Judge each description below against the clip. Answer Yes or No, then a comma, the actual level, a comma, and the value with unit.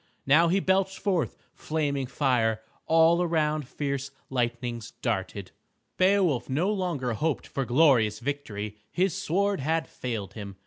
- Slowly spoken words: Yes, slow, 130 wpm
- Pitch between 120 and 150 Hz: Yes, medium, 140 Hz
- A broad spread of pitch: Yes, wide, 5.9 semitones